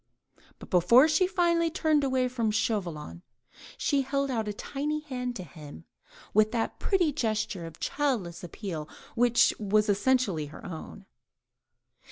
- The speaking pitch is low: No, high, 230 Hz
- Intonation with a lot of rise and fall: Yes, wide, 7.1 semitones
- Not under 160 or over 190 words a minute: No, average, 145 wpm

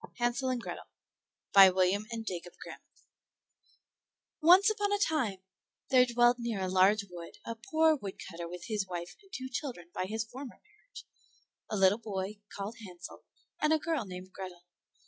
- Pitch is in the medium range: No, high, 215 Hz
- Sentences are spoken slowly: No, average, 165 wpm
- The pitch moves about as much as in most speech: No, wide, 5.8 semitones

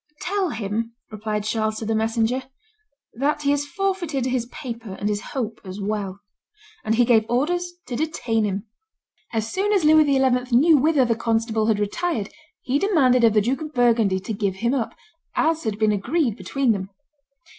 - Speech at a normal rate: Yes, average, 180 wpm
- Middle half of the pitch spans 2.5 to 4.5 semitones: No, average, 4.9 semitones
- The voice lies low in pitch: No, high, 235 Hz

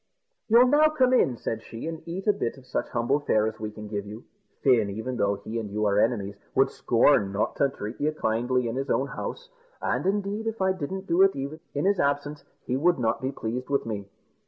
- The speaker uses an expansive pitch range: Yes, wide, 7.8 semitones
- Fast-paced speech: Yes, fast, 230 wpm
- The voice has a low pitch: Yes, low, 130 Hz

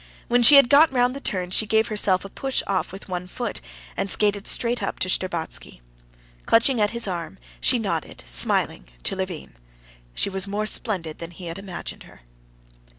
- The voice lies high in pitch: Yes, high, 195 Hz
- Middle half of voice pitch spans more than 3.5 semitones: Yes, average, 4.4 semitones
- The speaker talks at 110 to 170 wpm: No, average, 185 wpm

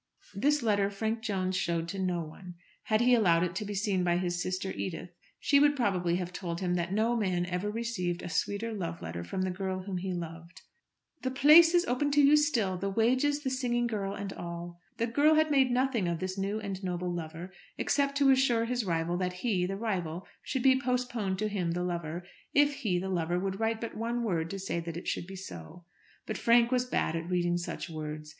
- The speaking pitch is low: No, high, 195 Hz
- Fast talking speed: Yes, fast, 220 wpm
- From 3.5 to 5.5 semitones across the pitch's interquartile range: Yes, average, 5.2 semitones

